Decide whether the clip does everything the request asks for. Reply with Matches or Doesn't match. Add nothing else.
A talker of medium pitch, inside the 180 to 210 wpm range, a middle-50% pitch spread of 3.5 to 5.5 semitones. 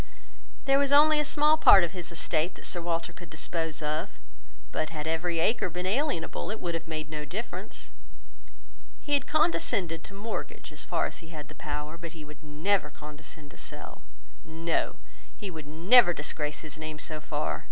Matches